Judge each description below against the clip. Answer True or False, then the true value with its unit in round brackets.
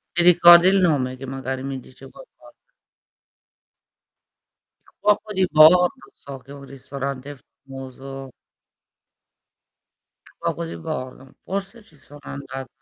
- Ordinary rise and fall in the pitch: True (4.5 semitones)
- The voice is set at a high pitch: False (140 Hz)